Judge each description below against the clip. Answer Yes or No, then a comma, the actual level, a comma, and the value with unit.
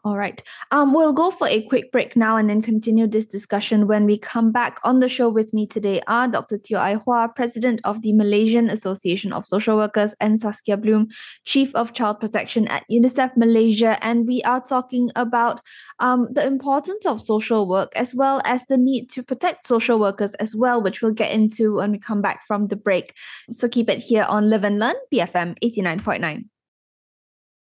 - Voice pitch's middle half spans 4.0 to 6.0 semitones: No, average, 2.7 semitones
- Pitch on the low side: No, high, 225 Hz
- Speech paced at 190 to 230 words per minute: Yes, average, 200 wpm